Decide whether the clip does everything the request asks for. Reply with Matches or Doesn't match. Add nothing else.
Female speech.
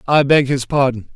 Doesn't match